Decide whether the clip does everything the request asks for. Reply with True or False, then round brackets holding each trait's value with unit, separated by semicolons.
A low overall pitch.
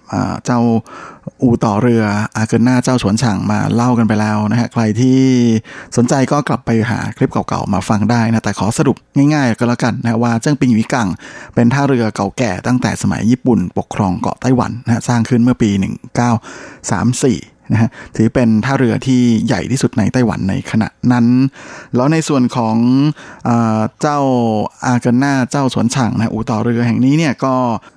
True (120 Hz)